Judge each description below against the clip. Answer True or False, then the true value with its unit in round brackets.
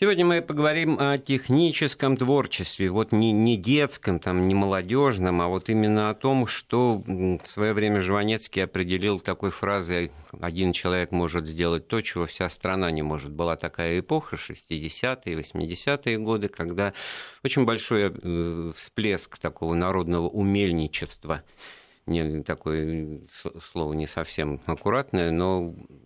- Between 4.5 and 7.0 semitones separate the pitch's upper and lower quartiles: True (4.9 semitones)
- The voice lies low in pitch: True (95 Hz)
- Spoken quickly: False (125 wpm)